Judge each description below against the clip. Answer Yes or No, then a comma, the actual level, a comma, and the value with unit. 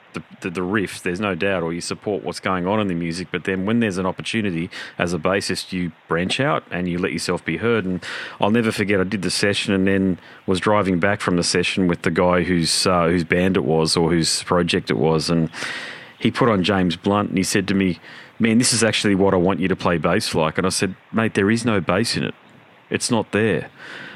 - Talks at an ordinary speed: No, fast, 250 wpm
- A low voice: Yes, very low, 95 Hz